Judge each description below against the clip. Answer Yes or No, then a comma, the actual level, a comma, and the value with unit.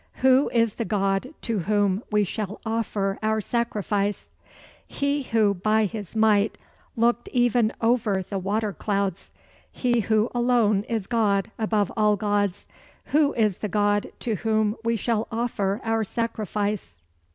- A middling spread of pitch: No, narrow, 2.2 semitones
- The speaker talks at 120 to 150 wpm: Yes, average, 140 wpm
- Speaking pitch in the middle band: No, high, 215 Hz